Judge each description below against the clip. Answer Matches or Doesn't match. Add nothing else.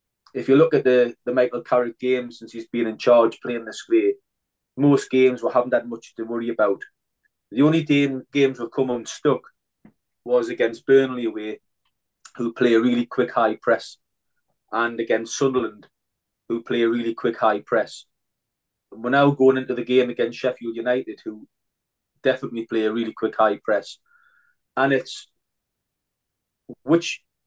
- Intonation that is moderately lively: Doesn't match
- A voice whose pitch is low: Matches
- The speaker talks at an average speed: Matches